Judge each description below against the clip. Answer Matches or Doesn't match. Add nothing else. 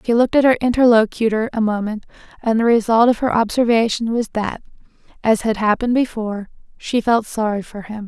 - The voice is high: Matches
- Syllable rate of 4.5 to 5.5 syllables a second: Doesn't match